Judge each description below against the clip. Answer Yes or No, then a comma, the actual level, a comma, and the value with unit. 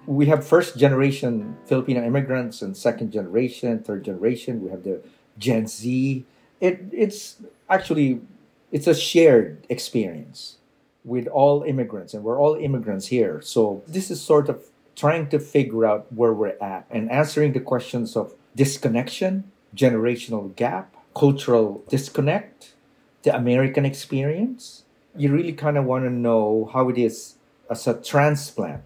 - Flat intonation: No, average, 4.1 semitones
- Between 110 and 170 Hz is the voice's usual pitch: Yes, low, 135 Hz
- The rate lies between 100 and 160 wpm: Yes, average, 145 wpm